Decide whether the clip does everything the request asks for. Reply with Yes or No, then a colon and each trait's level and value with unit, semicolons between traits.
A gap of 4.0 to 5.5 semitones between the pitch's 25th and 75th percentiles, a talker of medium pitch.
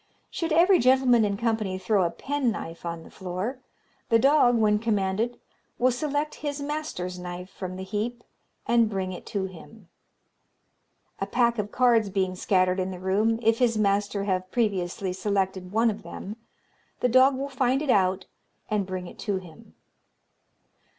No: average, 4.5 semitones; high, 210 Hz